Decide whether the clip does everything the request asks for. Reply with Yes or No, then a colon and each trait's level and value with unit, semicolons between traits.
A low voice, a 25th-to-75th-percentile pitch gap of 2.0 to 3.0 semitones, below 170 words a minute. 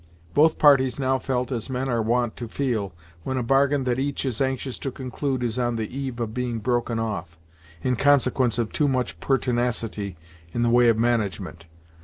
No: low, 125 Hz; narrow, 2.4 semitones; average, 190 wpm